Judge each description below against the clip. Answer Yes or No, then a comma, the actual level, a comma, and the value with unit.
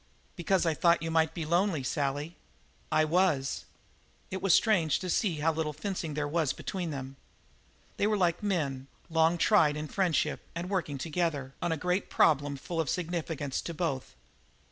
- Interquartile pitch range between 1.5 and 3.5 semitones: Yes, average, 3.2 semitones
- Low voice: No, medium, 160 Hz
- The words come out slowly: No, average, 170 wpm